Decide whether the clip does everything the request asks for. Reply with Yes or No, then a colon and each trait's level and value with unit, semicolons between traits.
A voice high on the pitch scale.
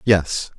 No: very low, 90 Hz